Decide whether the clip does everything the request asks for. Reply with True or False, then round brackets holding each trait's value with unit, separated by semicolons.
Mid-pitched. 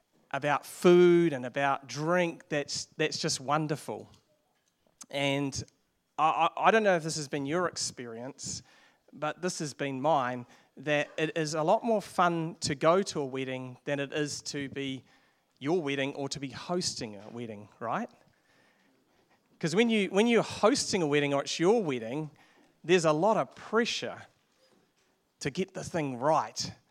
True (150 Hz)